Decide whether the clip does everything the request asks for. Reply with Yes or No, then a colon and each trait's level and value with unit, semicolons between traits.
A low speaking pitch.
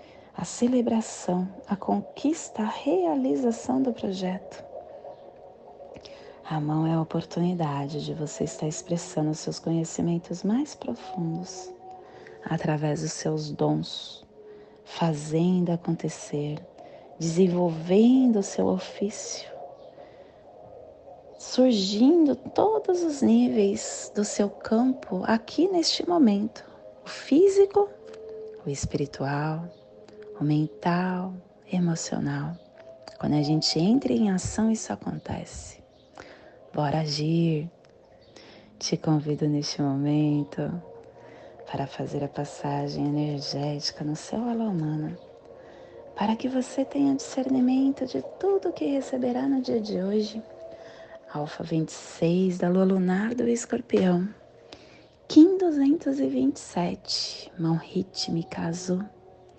No: medium, 185 Hz